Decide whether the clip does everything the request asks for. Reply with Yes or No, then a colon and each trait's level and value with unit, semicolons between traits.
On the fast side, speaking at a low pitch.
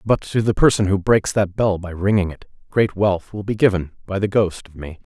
Yes: fast, 245 wpm; low, 100 Hz